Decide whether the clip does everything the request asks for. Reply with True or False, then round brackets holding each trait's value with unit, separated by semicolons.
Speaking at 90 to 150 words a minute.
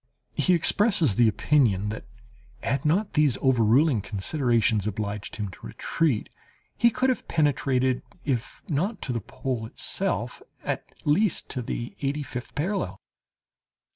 True (135 wpm)